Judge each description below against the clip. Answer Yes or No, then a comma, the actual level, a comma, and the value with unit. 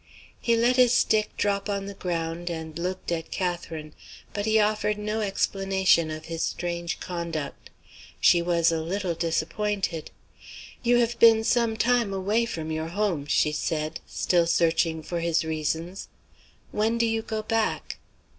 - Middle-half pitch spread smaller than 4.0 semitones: No, average, 4.5 semitones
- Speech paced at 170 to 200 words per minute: No, average, 155 wpm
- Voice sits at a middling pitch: Yes, medium, 180 Hz